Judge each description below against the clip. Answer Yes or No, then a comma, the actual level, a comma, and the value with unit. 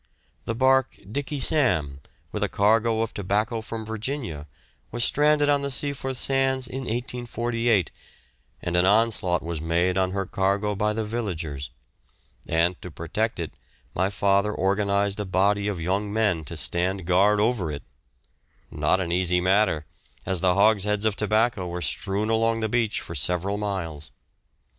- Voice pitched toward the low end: Yes, low, 100 Hz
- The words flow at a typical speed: Yes, average, 155 wpm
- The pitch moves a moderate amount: Yes, average, 4.1 semitones